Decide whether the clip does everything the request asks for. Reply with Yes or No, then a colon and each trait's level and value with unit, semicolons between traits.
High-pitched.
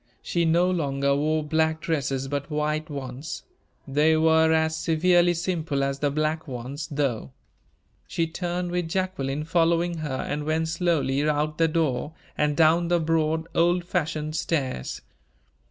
No: medium, 155 Hz